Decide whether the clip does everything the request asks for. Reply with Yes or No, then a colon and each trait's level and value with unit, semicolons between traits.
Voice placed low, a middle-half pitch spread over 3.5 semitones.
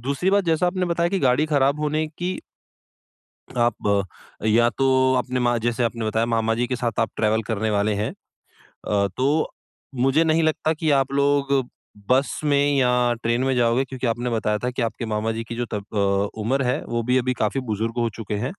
Yes: low, 125 Hz; average, 3.9 semitones